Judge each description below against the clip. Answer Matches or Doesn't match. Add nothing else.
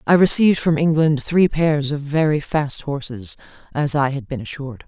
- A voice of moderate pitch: Matches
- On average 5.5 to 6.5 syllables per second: Doesn't match